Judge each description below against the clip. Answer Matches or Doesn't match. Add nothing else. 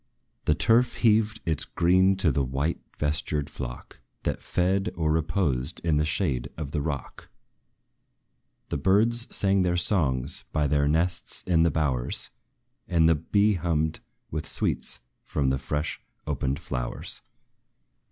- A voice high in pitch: Doesn't match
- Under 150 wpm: Matches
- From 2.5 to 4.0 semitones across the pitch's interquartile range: Doesn't match